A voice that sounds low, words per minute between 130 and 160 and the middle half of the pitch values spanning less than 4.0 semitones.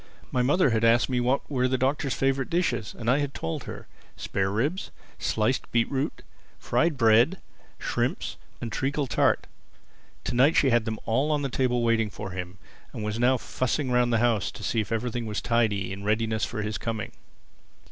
No: low, 120 Hz; average, 200 wpm; average, 3.5 semitones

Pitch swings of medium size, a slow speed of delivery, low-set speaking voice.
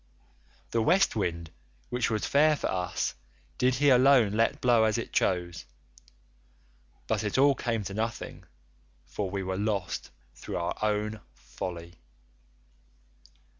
Yes: average, 5.0 semitones; slow, 130 wpm; low, 110 Hz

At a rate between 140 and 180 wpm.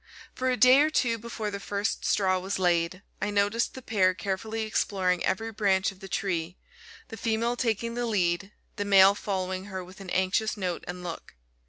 No: average, 190 wpm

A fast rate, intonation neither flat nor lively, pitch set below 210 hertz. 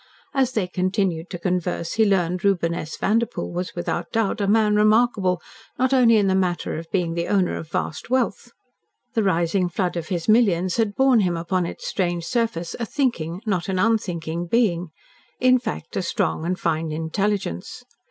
No: average, 180 wpm; average, 4.3 semitones; medium, 185 Hz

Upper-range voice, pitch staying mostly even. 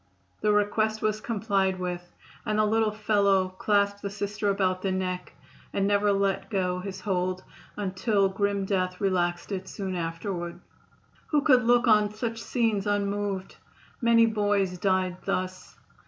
Yes: high, 200 Hz; narrow, 2.2 semitones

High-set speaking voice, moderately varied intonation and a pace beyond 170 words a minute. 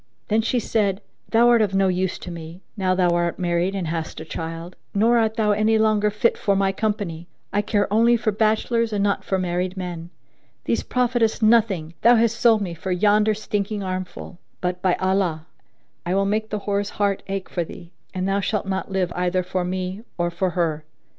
Yes: high, 195 Hz; average, 3.2 semitones; fast, 205 wpm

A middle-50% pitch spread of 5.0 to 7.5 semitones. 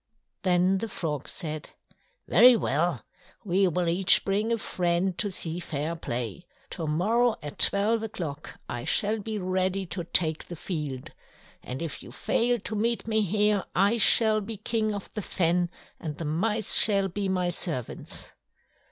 No: average, 4.3 semitones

